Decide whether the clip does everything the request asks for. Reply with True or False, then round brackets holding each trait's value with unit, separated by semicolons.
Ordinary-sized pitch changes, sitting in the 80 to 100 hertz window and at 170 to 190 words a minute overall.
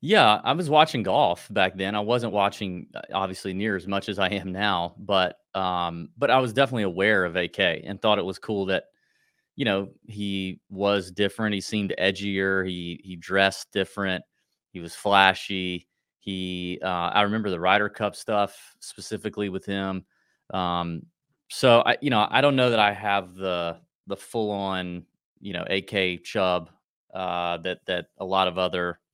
False (2.1 semitones; 95 Hz; 175 wpm)